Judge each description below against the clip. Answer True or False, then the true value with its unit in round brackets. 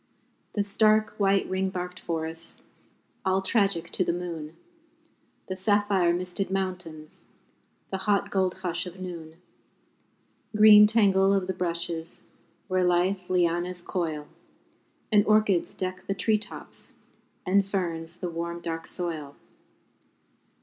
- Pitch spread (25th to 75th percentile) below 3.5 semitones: True (2.4 semitones)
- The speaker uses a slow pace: True (120 wpm)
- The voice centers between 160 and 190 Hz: True (185 Hz)